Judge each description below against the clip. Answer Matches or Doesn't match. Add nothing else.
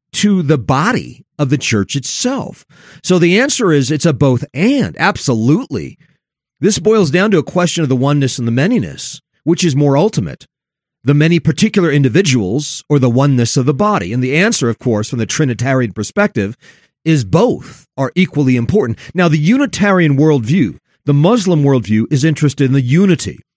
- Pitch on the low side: Doesn't match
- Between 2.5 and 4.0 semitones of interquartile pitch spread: Doesn't match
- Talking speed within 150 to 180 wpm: Matches